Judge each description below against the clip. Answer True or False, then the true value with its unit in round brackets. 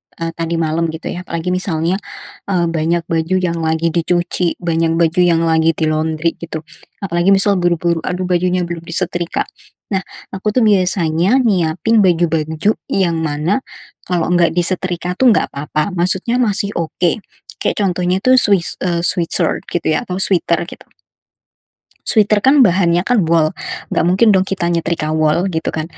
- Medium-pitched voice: True (175 Hz)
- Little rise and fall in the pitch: True (2.3 semitones)